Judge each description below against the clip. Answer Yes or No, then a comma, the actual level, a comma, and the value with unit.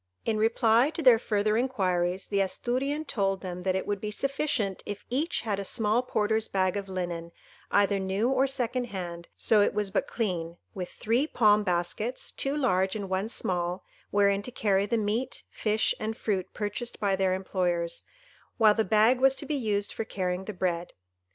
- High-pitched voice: Yes, high, 205 Hz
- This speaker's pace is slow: No, average, 185 wpm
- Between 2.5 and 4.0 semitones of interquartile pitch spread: Yes, average, 3.5 semitones